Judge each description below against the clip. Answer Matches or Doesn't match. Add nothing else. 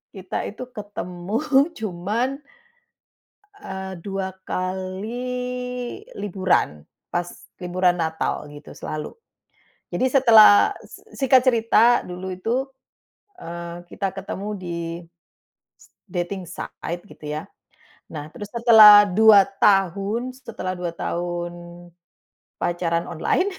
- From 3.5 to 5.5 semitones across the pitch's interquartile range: Matches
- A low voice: Doesn't match